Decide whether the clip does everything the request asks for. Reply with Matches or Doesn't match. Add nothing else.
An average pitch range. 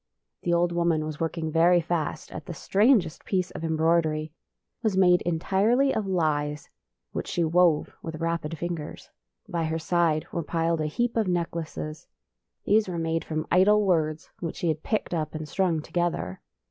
Doesn't match